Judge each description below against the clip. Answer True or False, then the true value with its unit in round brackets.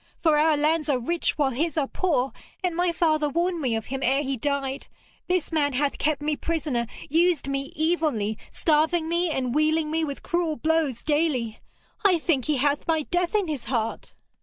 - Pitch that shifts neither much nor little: True (3.2 semitones)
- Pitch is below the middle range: False (305 Hz)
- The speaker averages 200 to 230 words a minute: False (190 wpm)